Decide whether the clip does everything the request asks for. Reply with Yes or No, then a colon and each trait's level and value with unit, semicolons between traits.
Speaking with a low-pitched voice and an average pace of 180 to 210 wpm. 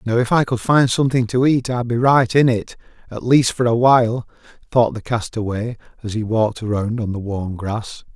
Yes: low, 115 Hz; fast, 205 wpm